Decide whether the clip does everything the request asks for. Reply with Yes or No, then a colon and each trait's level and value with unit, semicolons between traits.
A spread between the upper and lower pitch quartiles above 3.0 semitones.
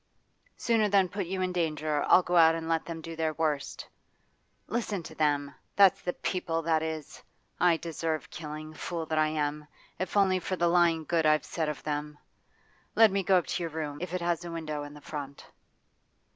No: narrow, 2.6 semitones